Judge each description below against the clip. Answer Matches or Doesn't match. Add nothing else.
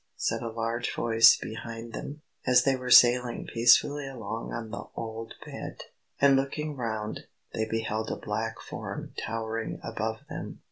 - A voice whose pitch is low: Matches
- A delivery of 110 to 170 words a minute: Matches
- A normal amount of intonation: Doesn't match